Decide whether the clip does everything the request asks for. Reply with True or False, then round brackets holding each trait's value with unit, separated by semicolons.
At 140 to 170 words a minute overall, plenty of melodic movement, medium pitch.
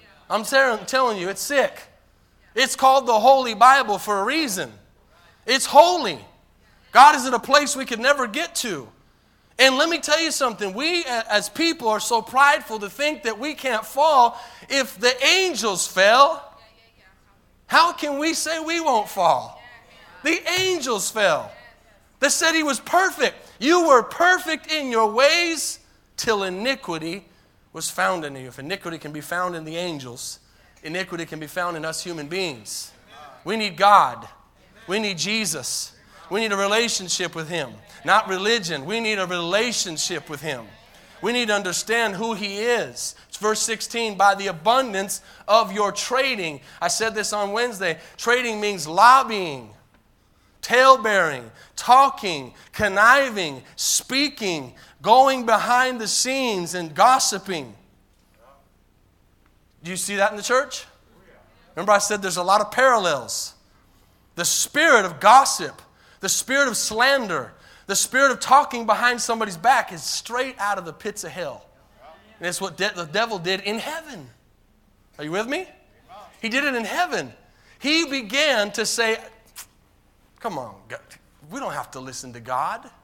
False (155 wpm; 6.8 semitones; 215 Hz)